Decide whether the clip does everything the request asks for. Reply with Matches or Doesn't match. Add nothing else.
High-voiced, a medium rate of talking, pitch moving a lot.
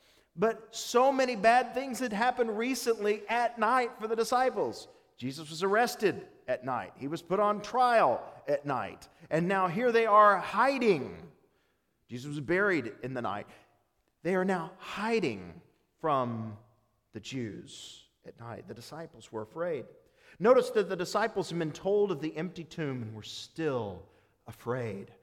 Matches